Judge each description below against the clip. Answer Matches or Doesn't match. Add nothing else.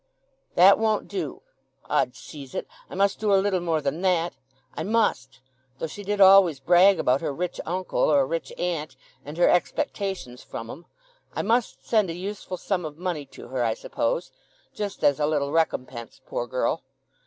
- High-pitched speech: Doesn't match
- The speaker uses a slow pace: Doesn't match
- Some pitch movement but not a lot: Doesn't match